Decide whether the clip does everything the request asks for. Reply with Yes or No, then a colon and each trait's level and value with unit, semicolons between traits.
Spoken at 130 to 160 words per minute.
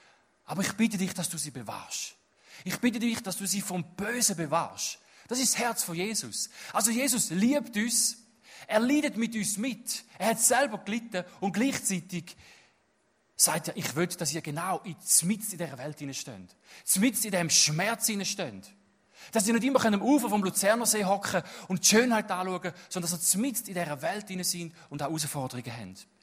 No: average, 185 wpm